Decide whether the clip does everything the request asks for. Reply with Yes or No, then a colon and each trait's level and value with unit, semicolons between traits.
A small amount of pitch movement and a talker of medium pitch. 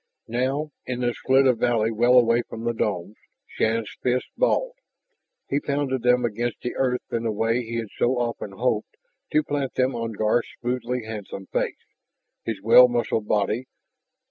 No: narrow, 2.1 semitones; low, 120 Hz